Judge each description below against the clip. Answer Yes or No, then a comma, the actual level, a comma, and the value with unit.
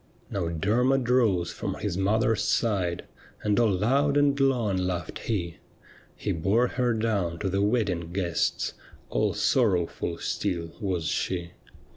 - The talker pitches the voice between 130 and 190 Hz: No, low, 100 Hz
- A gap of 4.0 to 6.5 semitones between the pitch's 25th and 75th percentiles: Yes, average, 5.1 semitones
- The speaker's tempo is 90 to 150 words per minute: Yes, average, 140 wpm